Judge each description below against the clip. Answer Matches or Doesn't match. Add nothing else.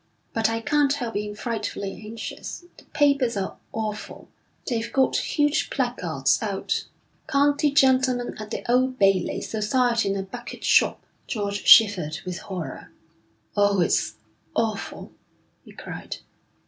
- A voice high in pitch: Matches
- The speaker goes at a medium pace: Doesn't match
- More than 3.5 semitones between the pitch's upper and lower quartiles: Matches